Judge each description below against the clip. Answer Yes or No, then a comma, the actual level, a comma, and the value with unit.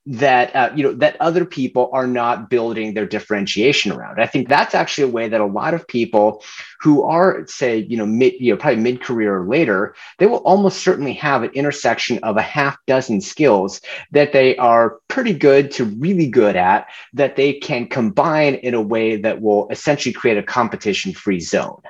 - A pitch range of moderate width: Yes, average, 4.4 semitones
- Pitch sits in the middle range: No, low, 125 Hz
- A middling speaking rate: Yes, average, 195 wpm